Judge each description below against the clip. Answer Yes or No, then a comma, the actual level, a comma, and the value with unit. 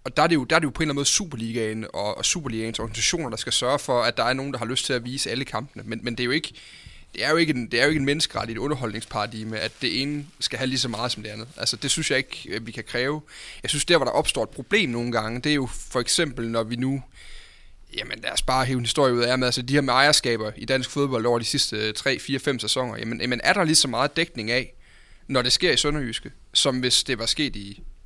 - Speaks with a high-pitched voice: No, low, 125 Hz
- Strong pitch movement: No, average, 3.8 semitones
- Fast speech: Yes, fast, 280 wpm